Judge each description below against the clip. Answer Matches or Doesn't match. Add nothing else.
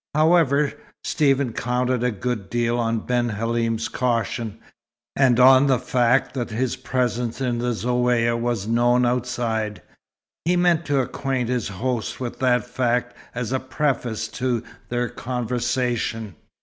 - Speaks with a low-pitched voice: Matches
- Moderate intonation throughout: Doesn't match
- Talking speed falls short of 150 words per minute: Matches